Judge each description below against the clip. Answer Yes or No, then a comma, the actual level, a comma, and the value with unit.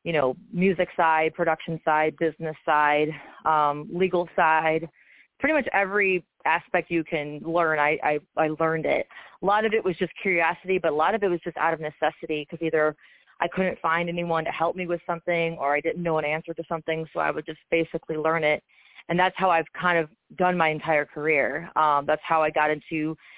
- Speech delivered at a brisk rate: Yes, fast, 210 wpm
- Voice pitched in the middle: Yes, medium, 165 Hz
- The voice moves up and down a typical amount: No, narrow, 2.2 semitones